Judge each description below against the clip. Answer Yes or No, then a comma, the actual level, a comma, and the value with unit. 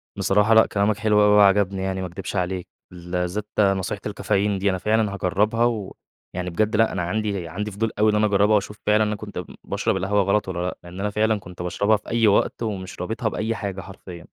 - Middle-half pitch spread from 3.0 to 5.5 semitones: No, narrow, 2.4 semitones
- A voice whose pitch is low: Yes, low, 100 Hz